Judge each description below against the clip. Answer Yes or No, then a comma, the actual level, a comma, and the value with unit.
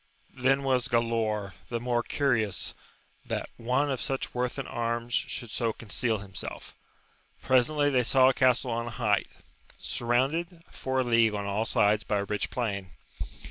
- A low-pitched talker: Yes, low, 120 Hz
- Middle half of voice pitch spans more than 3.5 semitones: No, average, 3.1 semitones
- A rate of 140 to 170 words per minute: Yes, average, 165 wpm